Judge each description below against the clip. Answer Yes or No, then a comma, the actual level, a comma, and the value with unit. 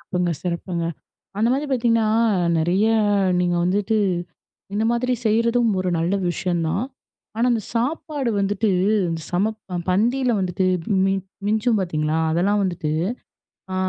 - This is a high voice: Yes, high, 200 Hz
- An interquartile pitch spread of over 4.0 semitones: Yes, average, 4.5 semitones